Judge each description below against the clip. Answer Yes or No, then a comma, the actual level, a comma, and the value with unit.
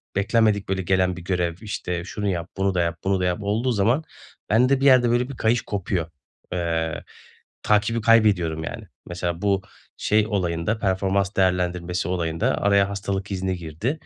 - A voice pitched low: Yes, very low, 95 Hz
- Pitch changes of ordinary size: Yes, average, 3.2 semitones